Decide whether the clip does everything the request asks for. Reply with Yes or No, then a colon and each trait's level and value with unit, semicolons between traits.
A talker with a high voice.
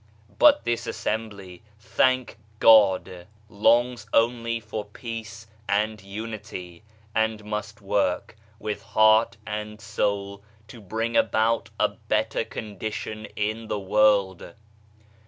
No: low, 110 Hz